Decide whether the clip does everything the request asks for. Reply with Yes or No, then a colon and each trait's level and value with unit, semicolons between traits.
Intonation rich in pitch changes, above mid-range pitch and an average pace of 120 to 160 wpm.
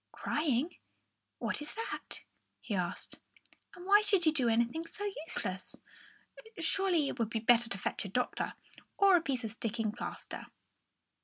Yes: wide, 7.1 semitones; very high, 255 Hz; average, 155 wpm